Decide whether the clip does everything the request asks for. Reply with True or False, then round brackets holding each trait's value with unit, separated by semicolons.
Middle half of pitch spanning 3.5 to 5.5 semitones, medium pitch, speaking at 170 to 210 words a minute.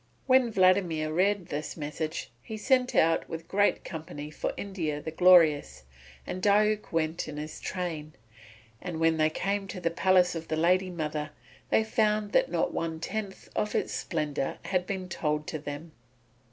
True (3.9 semitones; 170 Hz; 175 wpm)